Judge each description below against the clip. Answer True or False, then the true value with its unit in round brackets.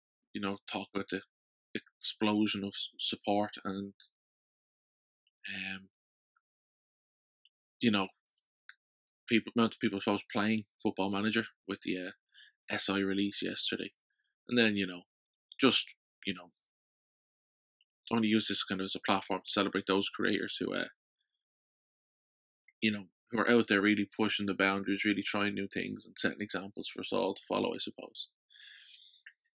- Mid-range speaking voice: False (100 Hz)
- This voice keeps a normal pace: True (145 wpm)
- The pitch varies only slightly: True (1.5 semitones)